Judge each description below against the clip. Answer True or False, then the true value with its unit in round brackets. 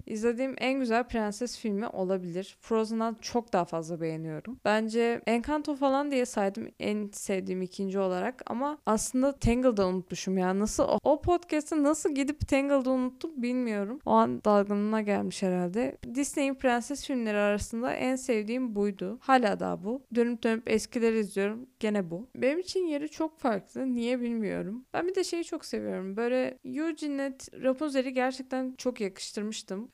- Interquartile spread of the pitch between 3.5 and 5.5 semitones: True (4.6 semitones)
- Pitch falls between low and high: False (235 Hz)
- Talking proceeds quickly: True (150 wpm)